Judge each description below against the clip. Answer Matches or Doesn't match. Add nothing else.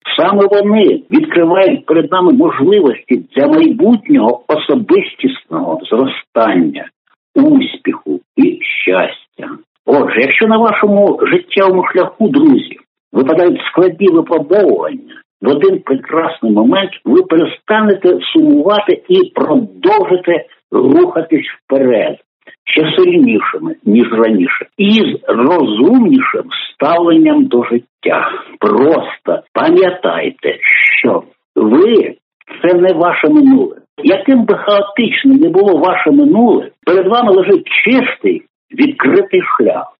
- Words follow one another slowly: Matches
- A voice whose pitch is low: Doesn't match